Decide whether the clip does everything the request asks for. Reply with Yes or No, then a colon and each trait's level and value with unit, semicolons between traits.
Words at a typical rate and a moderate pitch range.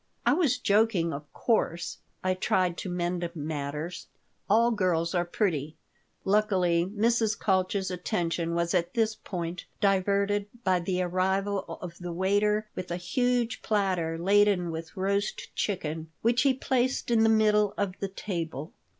Yes: average, 145 wpm; average, 3.5 semitones